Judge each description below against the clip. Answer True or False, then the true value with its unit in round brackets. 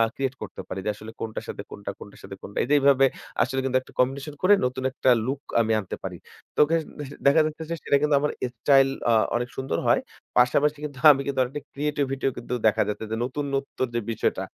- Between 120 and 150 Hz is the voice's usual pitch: True (135 Hz)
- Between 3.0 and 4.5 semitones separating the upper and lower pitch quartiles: False (2.6 semitones)